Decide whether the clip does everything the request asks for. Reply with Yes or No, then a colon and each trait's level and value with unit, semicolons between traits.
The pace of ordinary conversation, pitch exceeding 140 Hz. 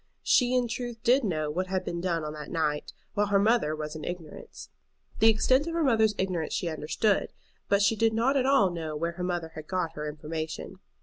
No: fast, 220 wpm; medium, 185 Hz